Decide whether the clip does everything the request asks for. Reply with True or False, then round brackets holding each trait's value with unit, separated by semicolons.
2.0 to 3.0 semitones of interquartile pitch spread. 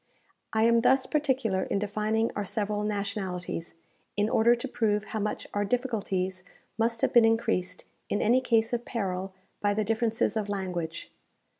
True (2.5 semitones)